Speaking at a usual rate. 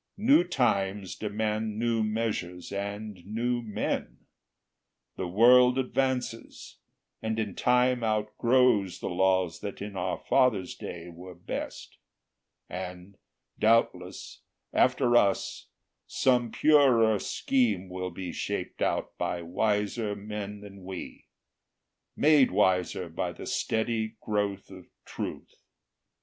No: slow, 110 wpm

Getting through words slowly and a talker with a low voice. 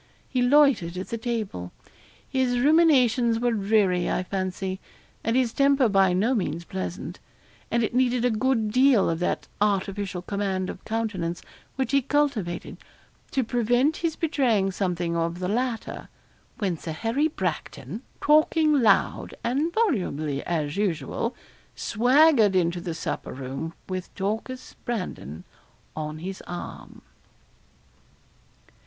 No: slow, 130 wpm; high, 215 Hz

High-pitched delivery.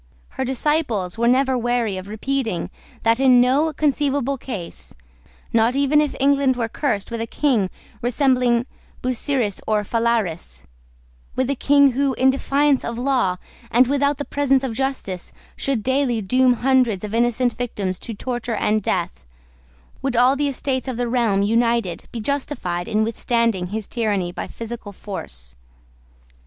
Yes: high, 240 Hz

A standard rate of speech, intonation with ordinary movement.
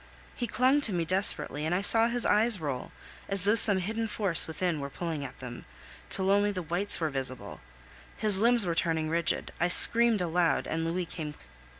Yes: average, 195 wpm; average, 4.5 semitones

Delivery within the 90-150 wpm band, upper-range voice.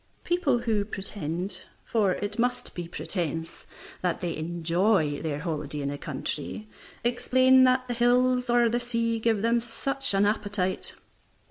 Yes: average, 145 wpm; high, 210 Hz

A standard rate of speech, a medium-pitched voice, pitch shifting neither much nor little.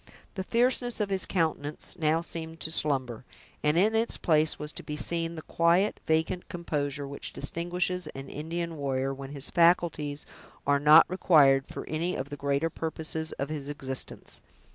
Yes: average, 165 wpm; medium, 160 Hz; average, 3.2 semitones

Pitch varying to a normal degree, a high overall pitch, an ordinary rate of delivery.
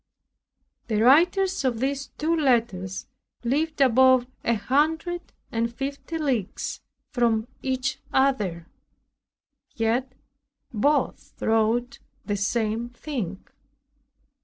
No: average, 4.0 semitones; very high, 250 Hz; slow, 90 wpm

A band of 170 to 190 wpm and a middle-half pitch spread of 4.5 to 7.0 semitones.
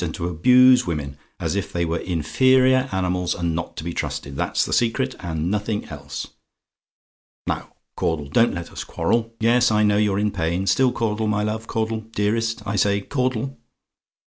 Yes: average, 175 wpm; average, 5.0 semitones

